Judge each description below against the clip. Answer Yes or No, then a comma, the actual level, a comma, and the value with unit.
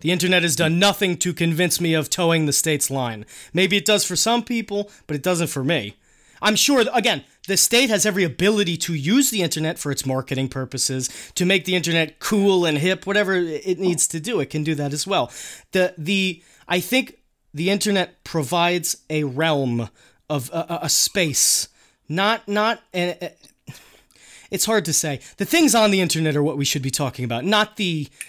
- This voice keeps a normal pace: Yes, average, 195 wpm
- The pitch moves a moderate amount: Yes, average, 4.7 semitones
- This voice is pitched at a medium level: Yes, medium, 175 Hz